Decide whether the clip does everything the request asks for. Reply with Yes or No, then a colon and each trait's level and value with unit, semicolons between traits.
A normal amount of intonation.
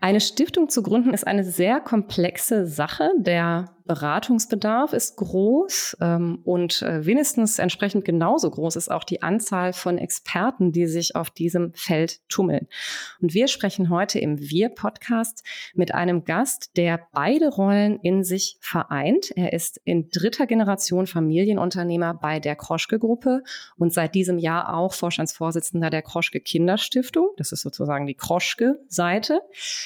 Yes: average, 4.7 semitones